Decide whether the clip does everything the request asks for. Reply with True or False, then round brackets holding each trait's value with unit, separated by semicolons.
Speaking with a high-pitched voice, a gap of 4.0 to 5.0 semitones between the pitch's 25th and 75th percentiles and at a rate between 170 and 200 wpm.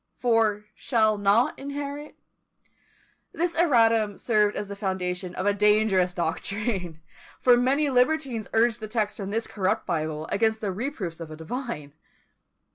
False (215 Hz; 4.4 semitones; 140 wpm)